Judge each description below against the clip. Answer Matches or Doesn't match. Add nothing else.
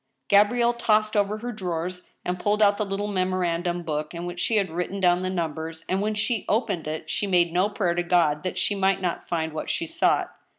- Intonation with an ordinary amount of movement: Matches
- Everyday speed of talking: Doesn't match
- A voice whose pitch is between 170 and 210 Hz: Matches